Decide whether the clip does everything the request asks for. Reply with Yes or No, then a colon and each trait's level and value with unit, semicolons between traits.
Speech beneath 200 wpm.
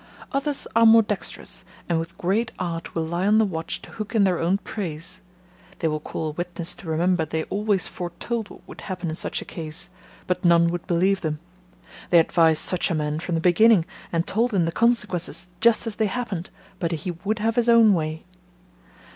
No: fast, 205 wpm